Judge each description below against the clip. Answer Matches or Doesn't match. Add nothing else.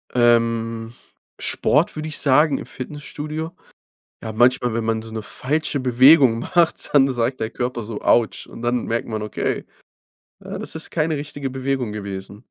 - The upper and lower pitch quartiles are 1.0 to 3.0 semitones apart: Doesn't match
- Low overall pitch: Matches